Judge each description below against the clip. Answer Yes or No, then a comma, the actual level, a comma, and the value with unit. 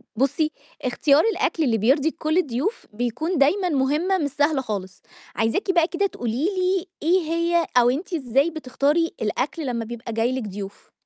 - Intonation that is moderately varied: No, wide, 5.7 semitones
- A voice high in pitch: Yes, very high, 285 Hz